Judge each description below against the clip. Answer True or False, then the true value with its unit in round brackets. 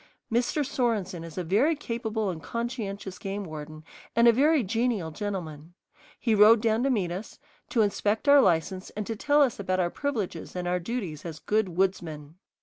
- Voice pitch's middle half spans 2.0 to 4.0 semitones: False (4.8 semitones)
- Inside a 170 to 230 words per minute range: True (180 wpm)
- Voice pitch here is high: True (205 Hz)